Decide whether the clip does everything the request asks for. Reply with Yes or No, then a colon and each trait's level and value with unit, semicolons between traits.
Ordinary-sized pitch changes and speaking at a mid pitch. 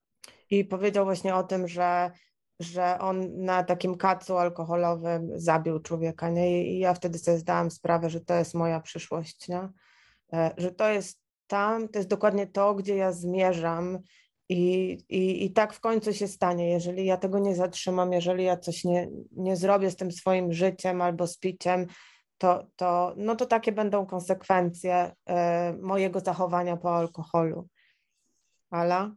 No: narrow, 1.6 semitones; medium, 180 Hz